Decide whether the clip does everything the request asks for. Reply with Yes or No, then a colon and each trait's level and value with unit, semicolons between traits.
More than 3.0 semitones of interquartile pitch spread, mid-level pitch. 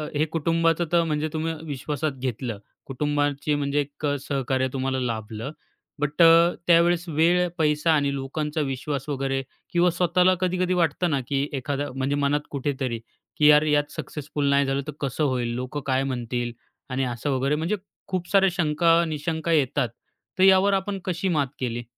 Yes: average, 3.6 semitones; medium, 145 Hz